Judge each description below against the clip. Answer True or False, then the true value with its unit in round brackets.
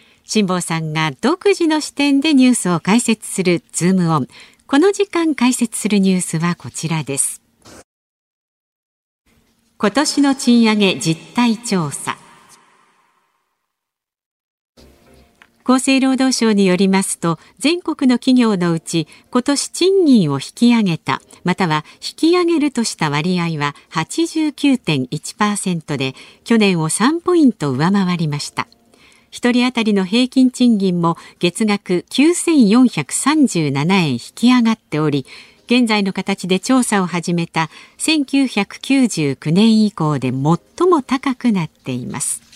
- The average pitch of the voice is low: False (210 Hz)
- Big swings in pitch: True (7.5 semitones)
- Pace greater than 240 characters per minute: False (235 characters per minute)